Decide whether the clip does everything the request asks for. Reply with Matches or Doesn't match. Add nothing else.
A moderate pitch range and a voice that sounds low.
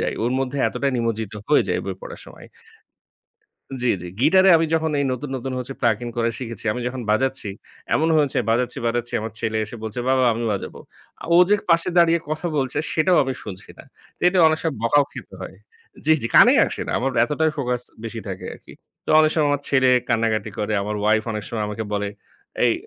Matches